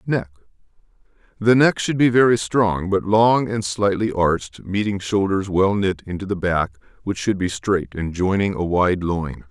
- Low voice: Yes, low, 100 Hz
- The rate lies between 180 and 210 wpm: No, average, 170 wpm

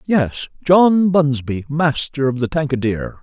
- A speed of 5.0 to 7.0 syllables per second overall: No, 4.1 syllables/s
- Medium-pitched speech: Yes, medium, 145 Hz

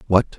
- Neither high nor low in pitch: No, low, 105 Hz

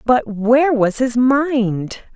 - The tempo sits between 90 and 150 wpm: Yes, average, 140 wpm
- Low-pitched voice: No, high, 240 Hz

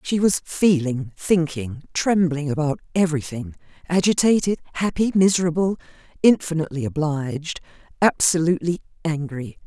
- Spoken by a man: No, female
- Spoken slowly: Yes, slow, 85 wpm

